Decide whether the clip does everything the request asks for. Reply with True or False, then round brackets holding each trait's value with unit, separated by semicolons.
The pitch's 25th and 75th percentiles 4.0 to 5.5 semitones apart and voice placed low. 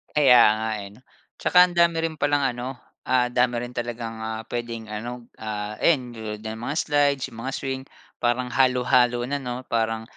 False (2.8 semitones; 120 Hz)